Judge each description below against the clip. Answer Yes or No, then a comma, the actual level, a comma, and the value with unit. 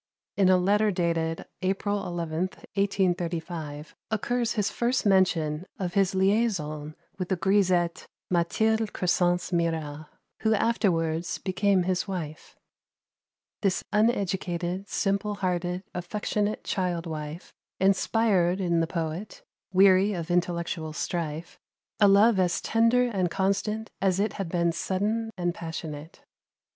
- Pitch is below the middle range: No, medium, 185 Hz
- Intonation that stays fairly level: No, average, 3.0 semitones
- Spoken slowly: Yes, slow, 120 wpm